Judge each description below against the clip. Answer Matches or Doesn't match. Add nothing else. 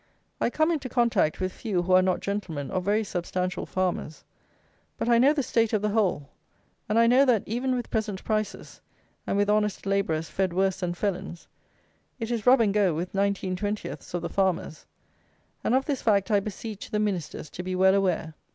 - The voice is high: Matches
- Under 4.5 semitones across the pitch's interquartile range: Matches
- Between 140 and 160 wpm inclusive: Doesn't match